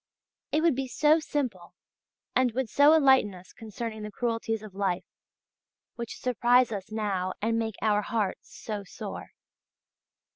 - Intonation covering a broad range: No, average, 3.6 semitones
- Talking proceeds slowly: No, average, 145 wpm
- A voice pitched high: Yes, high, 225 Hz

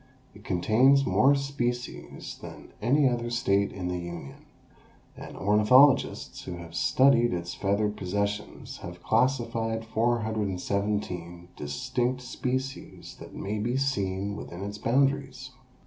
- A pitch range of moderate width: Yes, average, 4.6 semitones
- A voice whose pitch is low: Yes, low, 110 Hz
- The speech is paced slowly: Yes, slow, 115 wpm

